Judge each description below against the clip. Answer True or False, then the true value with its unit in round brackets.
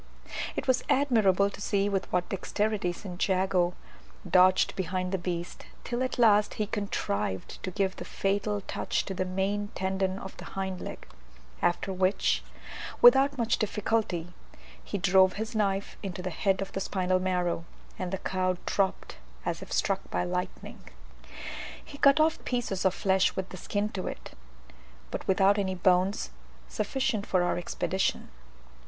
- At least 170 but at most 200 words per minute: False (160 wpm)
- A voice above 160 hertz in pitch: True (190 Hz)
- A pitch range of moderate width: False (1.9 semitones)